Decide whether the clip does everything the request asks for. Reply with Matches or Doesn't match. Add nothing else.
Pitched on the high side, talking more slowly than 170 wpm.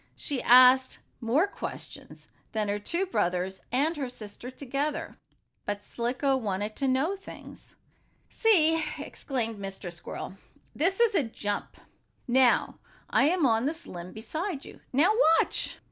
Matches